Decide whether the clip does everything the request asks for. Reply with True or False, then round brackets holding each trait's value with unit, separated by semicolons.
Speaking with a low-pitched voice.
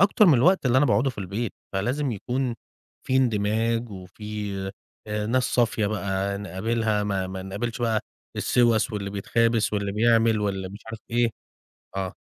True (110 Hz)